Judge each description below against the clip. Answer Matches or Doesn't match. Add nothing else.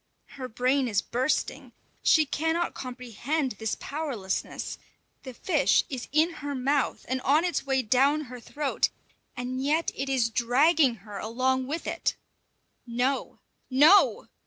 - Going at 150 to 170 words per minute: Doesn't match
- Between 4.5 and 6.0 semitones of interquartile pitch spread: Doesn't match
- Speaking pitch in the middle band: Doesn't match